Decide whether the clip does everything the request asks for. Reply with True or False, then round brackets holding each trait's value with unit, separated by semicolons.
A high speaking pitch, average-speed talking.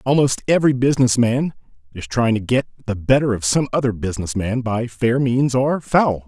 False (120 Hz; 180 wpm)